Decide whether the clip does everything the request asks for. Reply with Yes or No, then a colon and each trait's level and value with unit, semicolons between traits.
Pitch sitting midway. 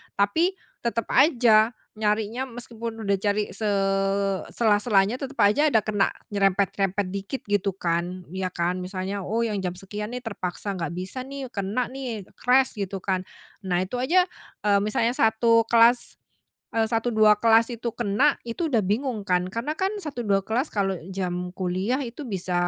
No: high, 215 Hz